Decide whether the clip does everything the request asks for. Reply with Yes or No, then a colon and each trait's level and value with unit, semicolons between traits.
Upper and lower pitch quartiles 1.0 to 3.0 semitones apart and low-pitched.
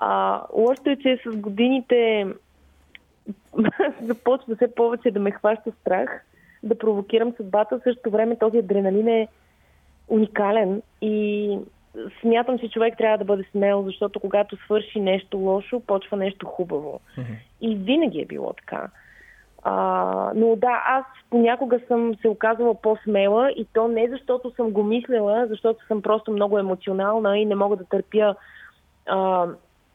No: narrow, 2.6 semitones; high, 215 Hz